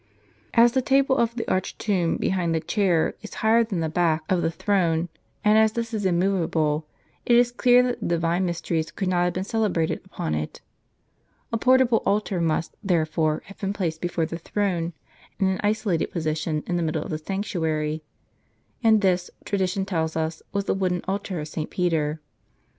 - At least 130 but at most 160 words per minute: No, average, 185 wpm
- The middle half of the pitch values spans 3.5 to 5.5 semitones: Yes, average, 4.2 semitones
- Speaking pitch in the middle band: Yes, medium, 180 Hz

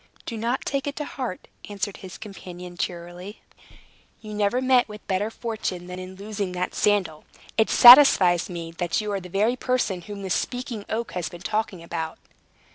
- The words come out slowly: No, average, 180 wpm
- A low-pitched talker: No, high, 200 Hz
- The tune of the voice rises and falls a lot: No, average, 3.9 semitones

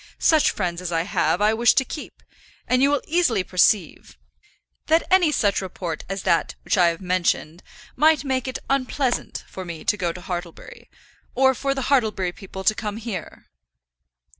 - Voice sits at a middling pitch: No, high, 210 Hz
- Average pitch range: No, wide, 6.8 semitones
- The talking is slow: No, average, 175 wpm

